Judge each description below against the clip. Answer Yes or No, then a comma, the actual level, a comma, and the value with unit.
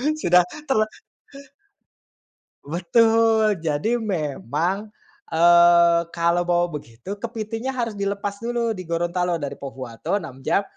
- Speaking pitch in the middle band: Yes, medium, 180 Hz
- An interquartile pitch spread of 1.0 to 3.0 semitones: No, average, 4.7 semitones